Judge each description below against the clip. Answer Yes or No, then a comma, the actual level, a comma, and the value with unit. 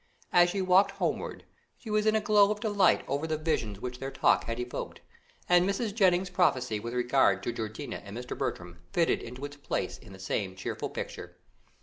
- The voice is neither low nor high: Yes, medium, 145 Hz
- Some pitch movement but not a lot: No, wide, 8.9 semitones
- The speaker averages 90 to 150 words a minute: No, average, 200 wpm